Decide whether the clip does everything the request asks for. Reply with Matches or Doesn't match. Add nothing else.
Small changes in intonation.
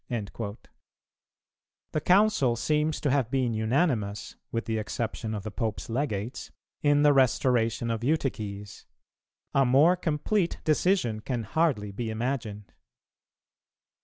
Doesn't match